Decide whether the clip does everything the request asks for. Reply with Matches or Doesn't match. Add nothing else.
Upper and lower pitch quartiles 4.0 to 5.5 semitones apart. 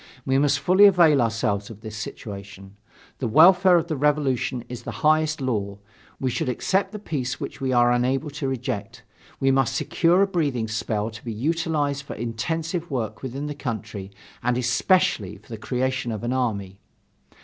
Matches